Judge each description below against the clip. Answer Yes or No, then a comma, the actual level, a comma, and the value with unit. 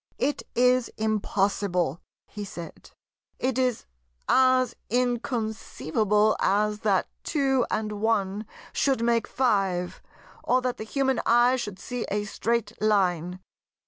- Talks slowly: Yes, slow, 115 wpm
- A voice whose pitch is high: Yes, high, 220 Hz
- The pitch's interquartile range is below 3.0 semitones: No, average, 3.6 semitones